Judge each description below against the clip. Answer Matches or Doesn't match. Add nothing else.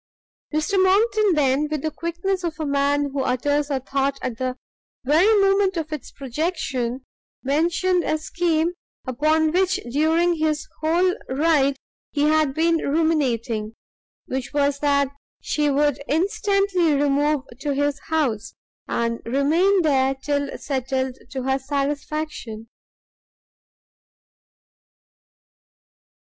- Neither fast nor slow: Doesn't match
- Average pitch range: Matches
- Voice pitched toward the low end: Doesn't match